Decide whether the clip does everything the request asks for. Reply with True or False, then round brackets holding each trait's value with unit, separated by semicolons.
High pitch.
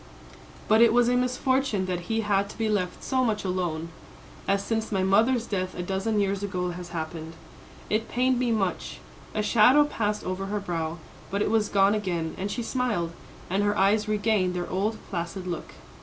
True (200 Hz)